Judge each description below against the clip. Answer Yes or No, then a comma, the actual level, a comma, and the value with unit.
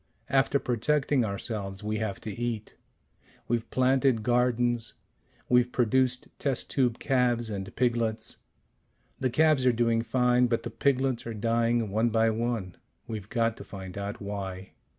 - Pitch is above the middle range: No, low, 115 Hz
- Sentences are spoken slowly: No, average, 145 wpm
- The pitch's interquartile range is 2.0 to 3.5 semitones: Yes, narrow, 2.5 semitones